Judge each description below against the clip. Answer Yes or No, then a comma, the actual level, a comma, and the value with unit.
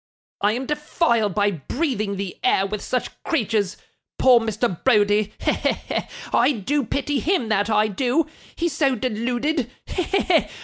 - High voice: Yes, high, 230 Hz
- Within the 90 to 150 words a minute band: Yes, average, 145 wpm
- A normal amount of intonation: Yes, average, 4.9 semitones